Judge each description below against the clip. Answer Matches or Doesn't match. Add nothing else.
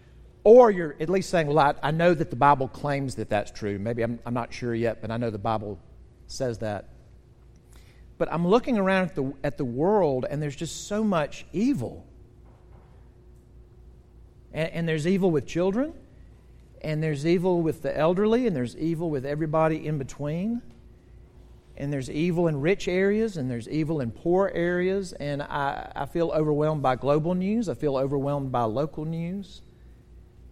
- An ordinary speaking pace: Matches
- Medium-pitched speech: Matches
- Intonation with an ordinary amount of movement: Matches